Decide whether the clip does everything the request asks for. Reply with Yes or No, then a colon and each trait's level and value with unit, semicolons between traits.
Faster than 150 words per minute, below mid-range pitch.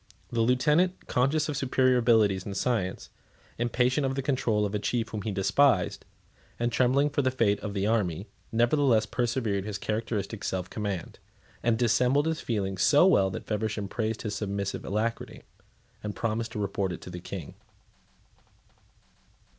Yes: average, 160 wpm; low, 110 Hz